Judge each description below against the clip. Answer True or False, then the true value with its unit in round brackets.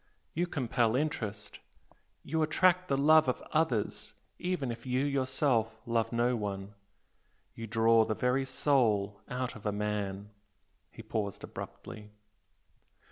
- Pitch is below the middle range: True (120 Hz)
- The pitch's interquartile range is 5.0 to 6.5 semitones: False (4.4 semitones)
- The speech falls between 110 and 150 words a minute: True (135 wpm)